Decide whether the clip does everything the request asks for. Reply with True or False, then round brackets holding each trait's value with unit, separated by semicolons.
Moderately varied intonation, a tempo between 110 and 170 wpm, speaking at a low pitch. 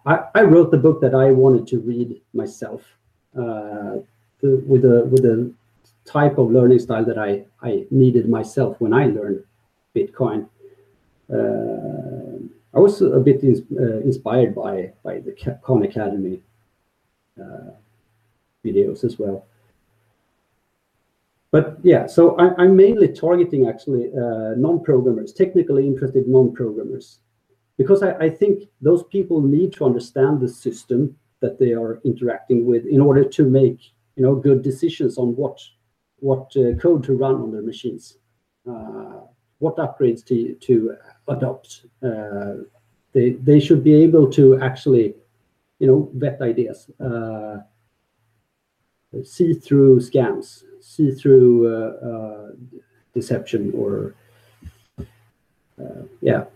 True (4.1 semitones; 135 wpm; 125 Hz)